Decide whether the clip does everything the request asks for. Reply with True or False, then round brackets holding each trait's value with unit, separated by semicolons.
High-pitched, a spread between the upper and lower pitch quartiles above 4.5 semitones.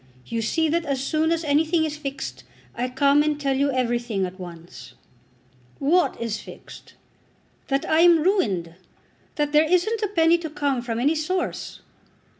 True (285 Hz; 5.2 semitones)